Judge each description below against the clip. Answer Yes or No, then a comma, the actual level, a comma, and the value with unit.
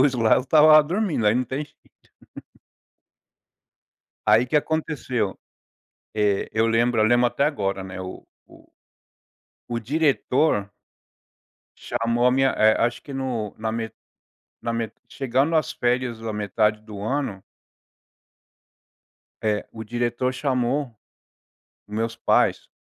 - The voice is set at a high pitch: No, low, 120 Hz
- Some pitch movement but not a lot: Yes, average, 3.6 semitones